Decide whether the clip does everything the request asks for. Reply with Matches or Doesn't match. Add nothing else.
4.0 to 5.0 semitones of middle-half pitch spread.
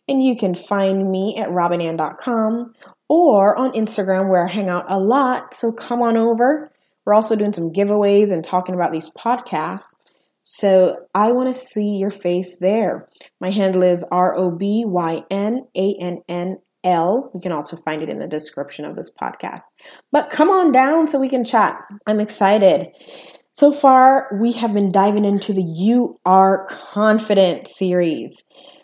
Matches